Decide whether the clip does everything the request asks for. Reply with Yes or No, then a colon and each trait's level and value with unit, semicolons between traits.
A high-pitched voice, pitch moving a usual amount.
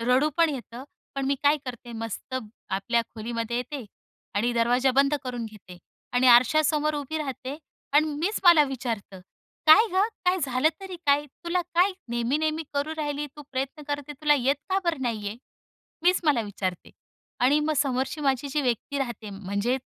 Yes: very high, 270 Hz; average, 4.1 semitones